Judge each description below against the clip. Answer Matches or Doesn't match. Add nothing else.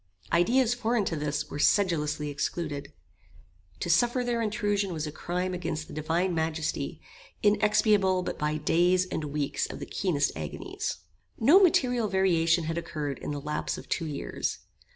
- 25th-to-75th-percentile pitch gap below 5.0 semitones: Doesn't match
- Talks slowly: Doesn't match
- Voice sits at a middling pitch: Matches